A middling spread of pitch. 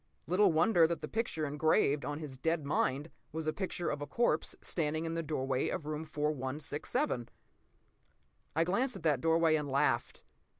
No: narrow, 2.3 semitones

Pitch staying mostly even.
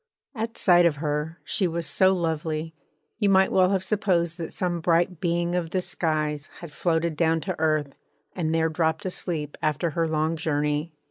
Yes: narrow, 2.3 semitones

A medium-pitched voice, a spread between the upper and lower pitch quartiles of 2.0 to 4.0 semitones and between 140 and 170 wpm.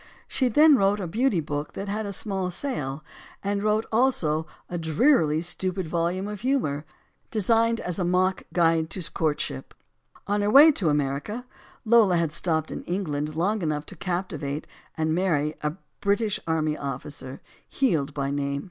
No: medium, 175 Hz; average, 5.3 semitones; average, 165 wpm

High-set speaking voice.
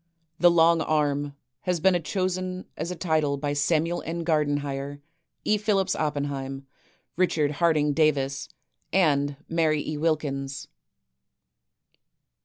No: medium, 155 Hz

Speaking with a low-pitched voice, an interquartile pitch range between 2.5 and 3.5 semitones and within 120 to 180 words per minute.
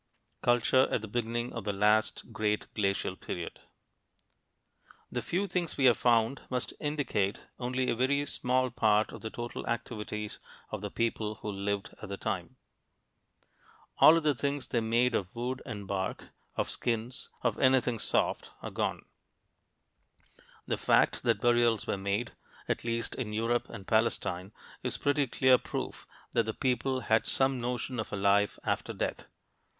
Yes: low, 115 Hz; average, 3.2 semitones; average, 160 wpm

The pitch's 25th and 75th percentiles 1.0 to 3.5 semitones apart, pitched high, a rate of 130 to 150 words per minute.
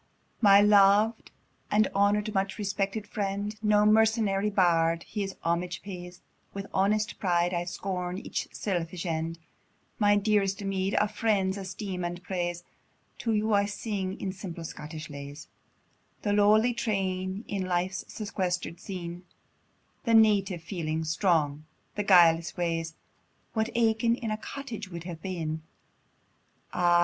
Yes: average, 3.1 semitones; high, 195 Hz; slow, 135 wpm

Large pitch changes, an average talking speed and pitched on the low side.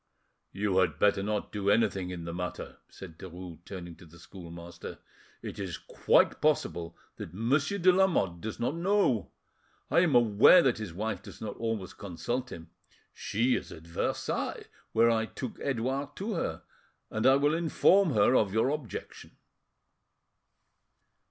Yes: wide, 6.8 semitones; average, 155 wpm; low, 110 Hz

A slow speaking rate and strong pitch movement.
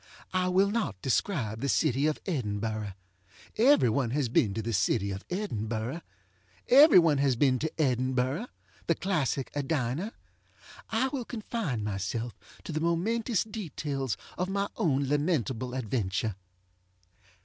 Yes: slow, 130 wpm; wide, 7.9 semitones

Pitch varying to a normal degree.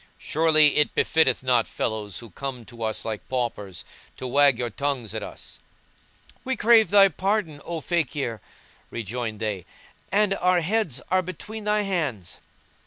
No: wide, 8.0 semitones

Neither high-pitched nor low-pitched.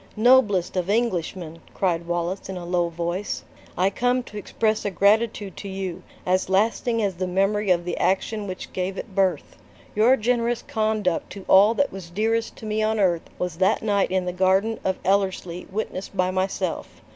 No: high, 195 Hz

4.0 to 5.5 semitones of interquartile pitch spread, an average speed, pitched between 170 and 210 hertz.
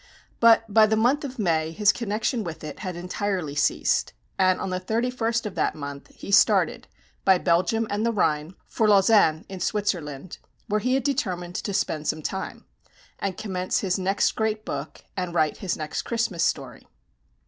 Yes: average, 4.5 semitones; average, 175 wpm; high, 190 Hz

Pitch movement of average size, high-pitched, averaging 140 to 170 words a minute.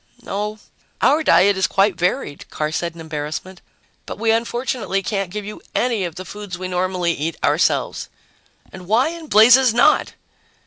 Yes: average, 4.1 semitones; high, 195 Hz; average, 165 wpm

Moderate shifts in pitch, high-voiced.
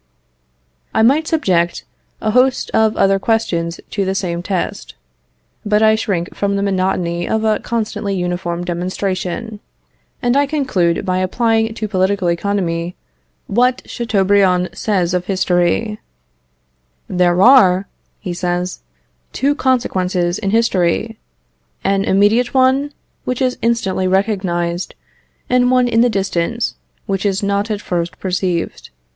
Yes: average, 3.9 semitones; high, 195 Hz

